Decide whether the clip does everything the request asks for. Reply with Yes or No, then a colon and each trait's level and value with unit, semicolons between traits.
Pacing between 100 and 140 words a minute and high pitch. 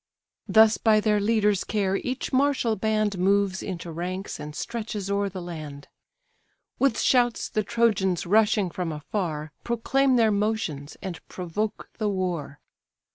Yes: slow, 135 wpm; high, 200 Hz